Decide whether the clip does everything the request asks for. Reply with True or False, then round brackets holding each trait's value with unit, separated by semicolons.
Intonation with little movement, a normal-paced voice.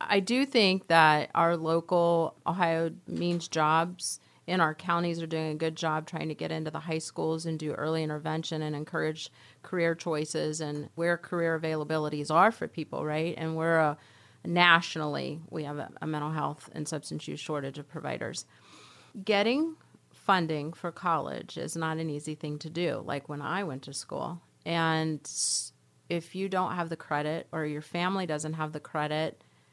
True (1.9 semitones; 175 wpm)